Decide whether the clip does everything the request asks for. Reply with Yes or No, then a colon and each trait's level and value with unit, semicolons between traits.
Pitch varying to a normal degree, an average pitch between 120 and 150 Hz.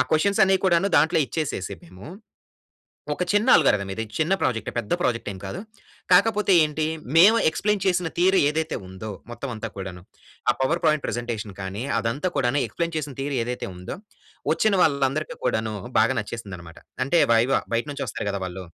No: wide, 7.5 semitones; medium, 140 Hz